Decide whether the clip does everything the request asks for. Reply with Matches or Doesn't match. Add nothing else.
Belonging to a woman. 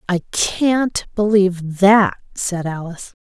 Matches